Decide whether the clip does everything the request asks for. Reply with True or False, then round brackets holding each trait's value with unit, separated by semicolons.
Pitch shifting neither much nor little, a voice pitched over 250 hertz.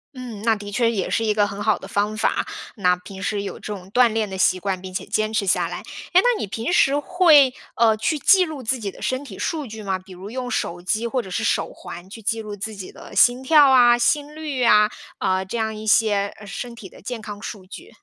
False (4.0 semitones; 220 Hz)